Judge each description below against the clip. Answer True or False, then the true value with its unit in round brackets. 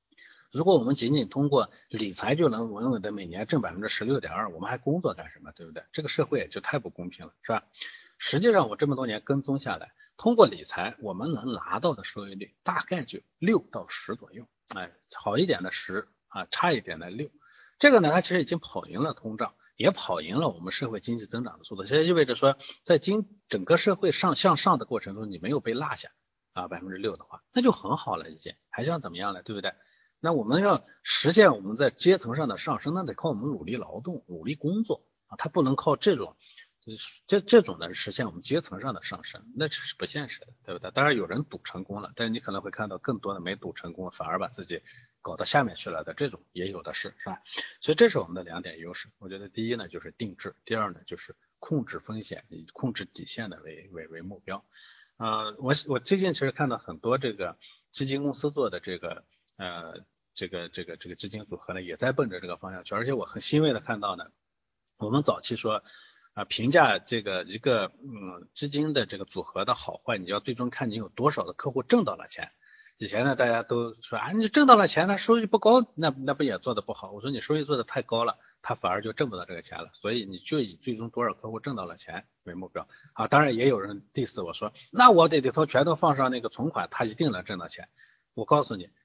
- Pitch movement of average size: False (7.1 semitones)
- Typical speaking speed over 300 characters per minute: True (340 characters per minute)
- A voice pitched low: True (130 Hz)